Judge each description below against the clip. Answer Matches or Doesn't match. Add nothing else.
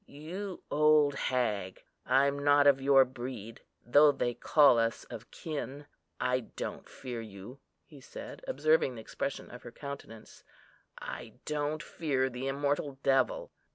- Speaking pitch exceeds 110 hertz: Matches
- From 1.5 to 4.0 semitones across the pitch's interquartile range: Matches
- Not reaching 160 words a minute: Matches